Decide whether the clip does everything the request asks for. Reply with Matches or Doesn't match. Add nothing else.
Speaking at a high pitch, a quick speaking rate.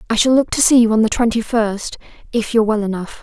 Matches